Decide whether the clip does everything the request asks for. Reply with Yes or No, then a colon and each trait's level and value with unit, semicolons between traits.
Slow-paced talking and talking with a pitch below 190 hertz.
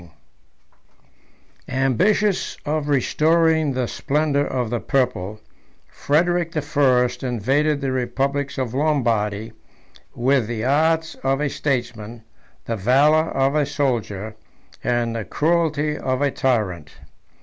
Yes: slow, 115 wpm; low, 135 Hz